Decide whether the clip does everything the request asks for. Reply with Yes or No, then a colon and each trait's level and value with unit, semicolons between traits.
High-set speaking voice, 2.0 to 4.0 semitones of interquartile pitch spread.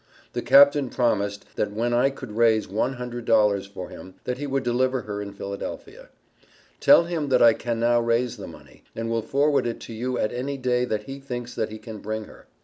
No: low, 120 Hz; average, 3.2 semitones